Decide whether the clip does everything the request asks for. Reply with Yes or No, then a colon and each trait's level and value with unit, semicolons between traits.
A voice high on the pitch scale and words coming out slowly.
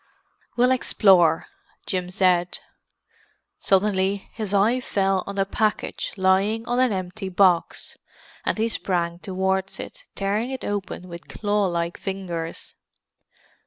Yes: high, 195 Hz; slow, 125 wpm